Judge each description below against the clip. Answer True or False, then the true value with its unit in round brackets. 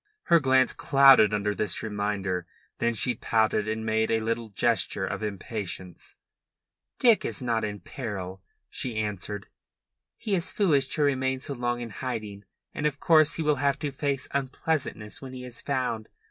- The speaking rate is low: False (165 wpm)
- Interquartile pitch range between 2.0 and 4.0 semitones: False (4.7 semitones)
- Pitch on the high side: False (120 Hz)